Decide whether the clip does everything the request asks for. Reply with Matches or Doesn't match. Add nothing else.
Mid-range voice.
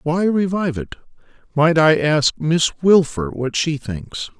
Matches